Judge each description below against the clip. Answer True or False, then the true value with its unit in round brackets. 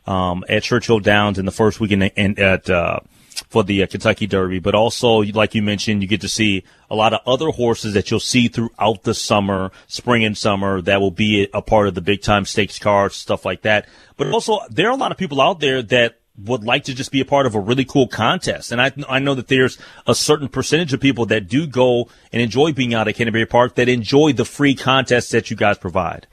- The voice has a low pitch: True (110 Hz)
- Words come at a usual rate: False (245 wpm)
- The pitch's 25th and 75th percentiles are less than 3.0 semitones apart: False (3.6 semitones)